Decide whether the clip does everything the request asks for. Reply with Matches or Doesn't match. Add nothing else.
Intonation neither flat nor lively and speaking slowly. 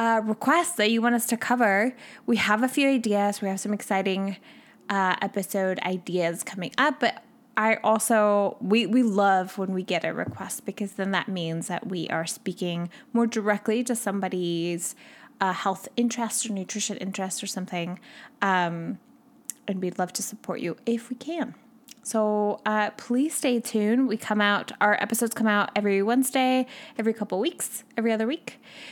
Doesn't match